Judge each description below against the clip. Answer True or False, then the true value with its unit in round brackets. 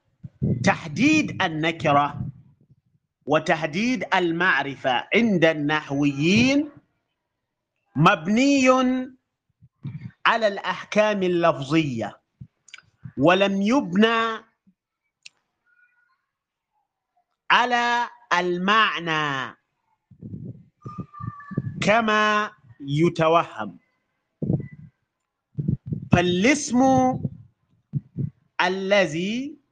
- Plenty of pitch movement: True (7.8 semitones)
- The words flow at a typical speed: False (35 wpm)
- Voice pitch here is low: False (185 Hz)